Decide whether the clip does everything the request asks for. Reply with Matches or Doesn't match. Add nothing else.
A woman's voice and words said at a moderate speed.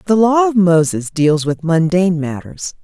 Matches